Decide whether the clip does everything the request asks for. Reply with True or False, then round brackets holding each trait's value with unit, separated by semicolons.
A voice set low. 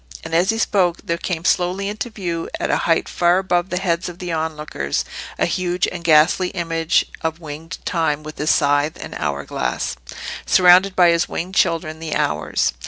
False (170 Hz)